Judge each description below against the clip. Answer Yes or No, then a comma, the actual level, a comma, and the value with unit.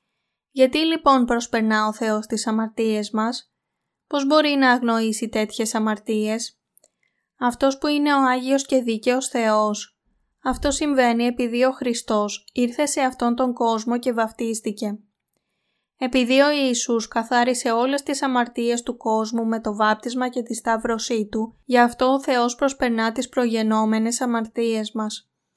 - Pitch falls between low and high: No, high, 235 Hz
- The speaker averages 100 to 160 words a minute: Yes, average, 140 wpm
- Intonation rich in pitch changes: No, narrow, 2.5 semitones